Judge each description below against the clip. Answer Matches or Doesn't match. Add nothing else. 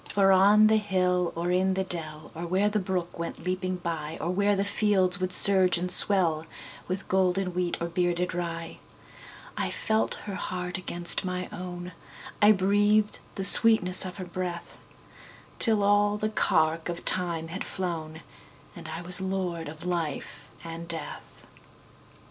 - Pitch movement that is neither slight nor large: Doesn't match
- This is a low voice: Doesn't match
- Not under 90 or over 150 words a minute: Matches